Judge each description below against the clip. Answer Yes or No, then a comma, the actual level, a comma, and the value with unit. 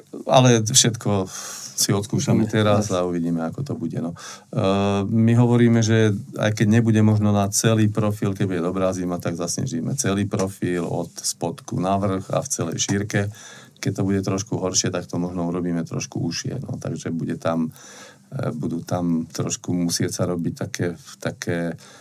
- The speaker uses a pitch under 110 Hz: Yes, low, 100 Hz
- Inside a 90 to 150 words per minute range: No, average, 160 wpm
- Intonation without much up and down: No, average, 3.7 semitones